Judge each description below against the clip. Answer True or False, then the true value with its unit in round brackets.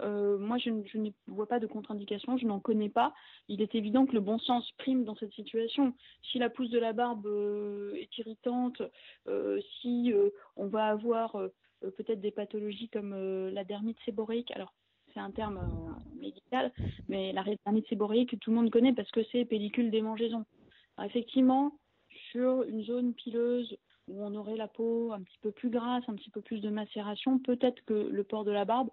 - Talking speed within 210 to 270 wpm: False (200 wpm)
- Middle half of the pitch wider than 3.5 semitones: False (2.5 semitones)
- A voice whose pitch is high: True (225 Hz)